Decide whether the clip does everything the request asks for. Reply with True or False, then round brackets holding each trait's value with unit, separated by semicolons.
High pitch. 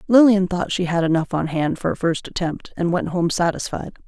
False (175 Hz)